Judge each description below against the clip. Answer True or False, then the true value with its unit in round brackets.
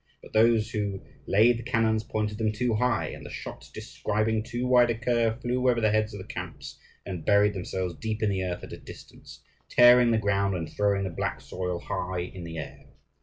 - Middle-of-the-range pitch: False (110 Hz)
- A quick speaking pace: True (215 wpm)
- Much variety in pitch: False (3.1 semitones)